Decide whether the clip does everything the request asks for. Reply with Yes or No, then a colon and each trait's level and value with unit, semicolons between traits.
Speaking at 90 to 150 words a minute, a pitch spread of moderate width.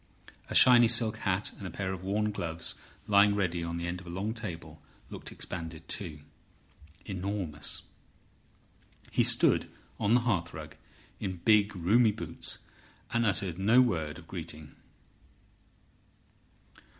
Yes: slow, 135 wpm; average, 4.0 semitones